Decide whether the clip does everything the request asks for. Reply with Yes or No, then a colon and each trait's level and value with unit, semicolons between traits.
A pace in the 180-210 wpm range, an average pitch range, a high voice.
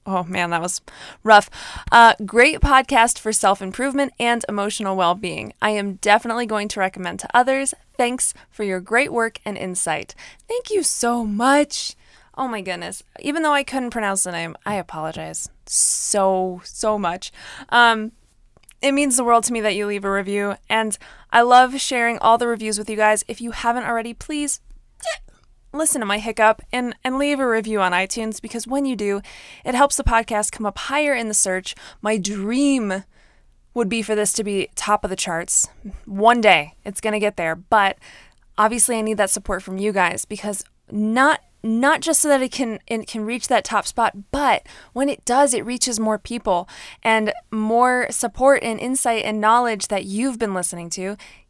Yes: average, 185 wpm; average, 3.5 semitones; high, 220 Hz